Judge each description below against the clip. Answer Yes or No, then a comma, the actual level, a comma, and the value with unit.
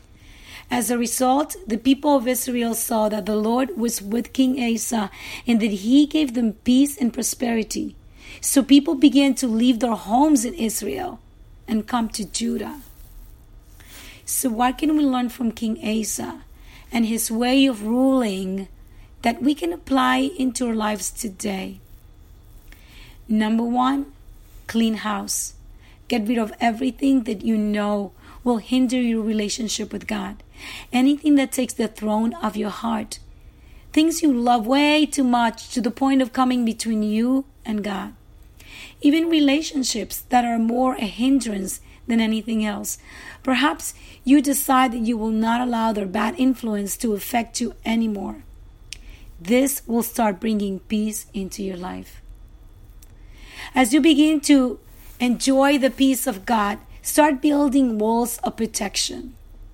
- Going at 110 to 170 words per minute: Yes, average, 145 wpm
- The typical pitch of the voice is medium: No, high, 230 Hz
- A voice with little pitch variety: No, average, 3.5 semitones